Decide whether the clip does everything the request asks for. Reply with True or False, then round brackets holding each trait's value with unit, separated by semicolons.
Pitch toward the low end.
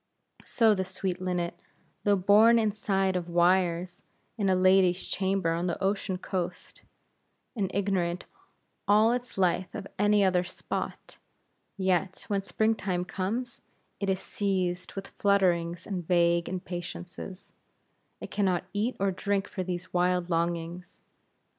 False (185 Hz)